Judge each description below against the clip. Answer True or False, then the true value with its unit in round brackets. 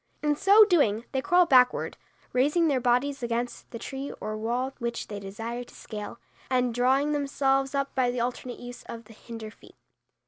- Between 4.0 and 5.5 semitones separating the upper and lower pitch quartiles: False (2.9 semitones)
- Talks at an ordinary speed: True (180 wpm)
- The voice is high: True (250 Hz)